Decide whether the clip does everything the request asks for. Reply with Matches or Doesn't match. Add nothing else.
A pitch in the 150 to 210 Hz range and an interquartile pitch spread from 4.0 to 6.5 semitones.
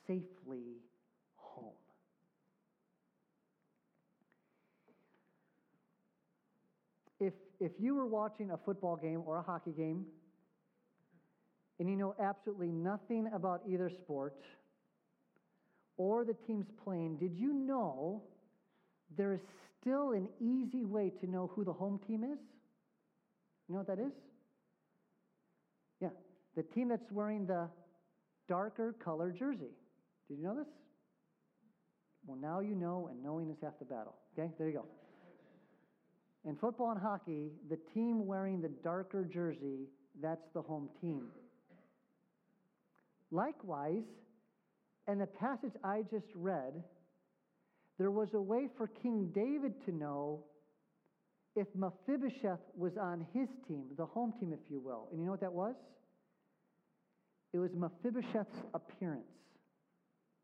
Matches